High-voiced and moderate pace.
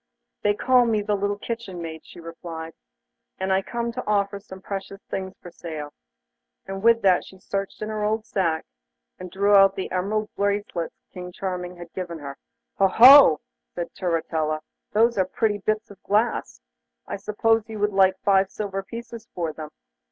Yes: high, 195 Hz; average, 175 wpm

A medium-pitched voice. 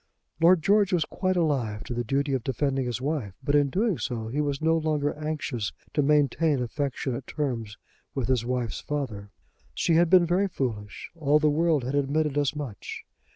Yes: medium, 145 Hz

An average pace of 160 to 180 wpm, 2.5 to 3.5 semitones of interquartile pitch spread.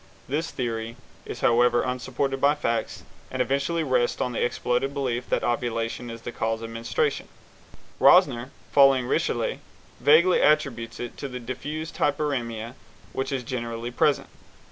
No: average, 145 wpm; average, 3.0 semitones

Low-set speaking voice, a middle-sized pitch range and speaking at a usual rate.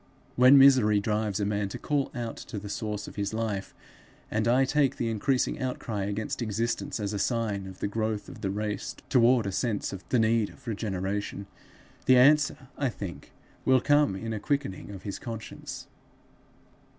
Yes: low, 110 Hz; average, 3.7 semitones; average, 180 wpm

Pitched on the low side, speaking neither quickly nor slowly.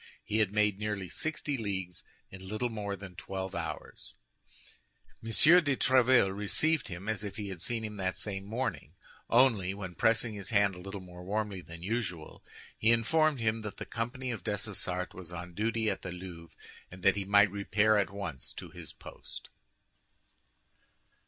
Yes: low, 100 Hz; average, 170 wpm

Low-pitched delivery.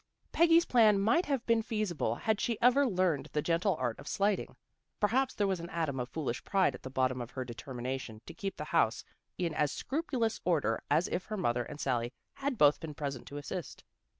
No: medium, 170 Hz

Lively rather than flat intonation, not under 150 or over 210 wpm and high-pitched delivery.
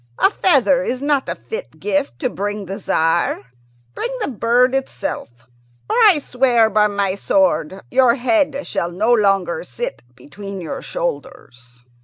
Yes: wide, 6.4 semitones; average, 155 wpm; high, 235 Hz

